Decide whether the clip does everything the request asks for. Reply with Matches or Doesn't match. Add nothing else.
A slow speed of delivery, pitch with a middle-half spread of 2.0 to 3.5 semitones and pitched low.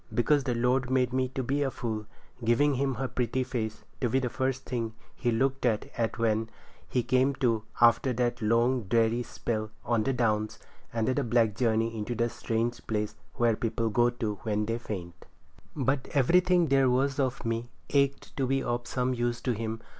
Doesn't match